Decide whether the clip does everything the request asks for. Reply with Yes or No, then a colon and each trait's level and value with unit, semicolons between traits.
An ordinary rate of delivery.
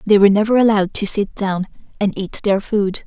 No: fast, 215 wpm